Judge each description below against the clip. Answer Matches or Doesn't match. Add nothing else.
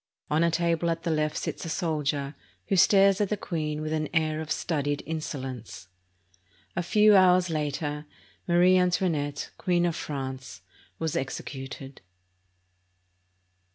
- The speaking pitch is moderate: Matches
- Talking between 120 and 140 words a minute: Matches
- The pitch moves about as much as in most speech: Matches